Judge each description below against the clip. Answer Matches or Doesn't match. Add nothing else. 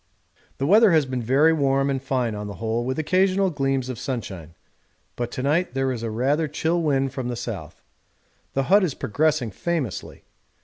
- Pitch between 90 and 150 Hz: Matches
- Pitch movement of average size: Matches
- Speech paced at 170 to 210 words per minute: Matches